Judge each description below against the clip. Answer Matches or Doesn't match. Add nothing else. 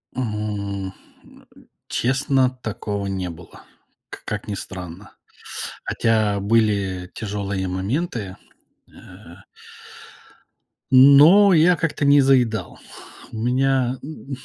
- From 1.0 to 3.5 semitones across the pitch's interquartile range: Doesn't match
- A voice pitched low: Matches